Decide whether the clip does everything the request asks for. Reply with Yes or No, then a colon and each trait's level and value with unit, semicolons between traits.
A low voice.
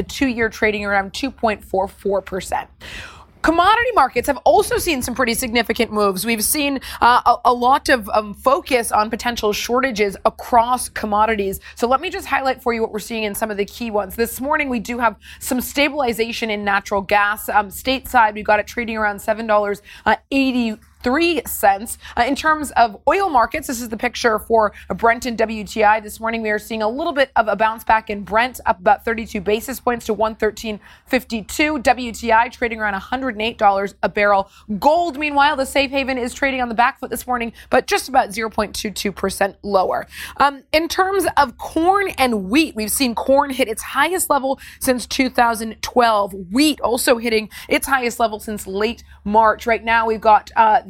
No: high, 235 Hz